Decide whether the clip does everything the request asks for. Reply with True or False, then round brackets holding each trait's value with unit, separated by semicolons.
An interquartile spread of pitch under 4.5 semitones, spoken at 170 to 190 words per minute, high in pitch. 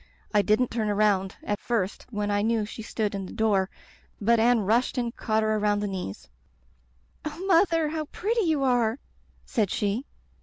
True (3.3 semitones; 180 wpm; 220 Hz)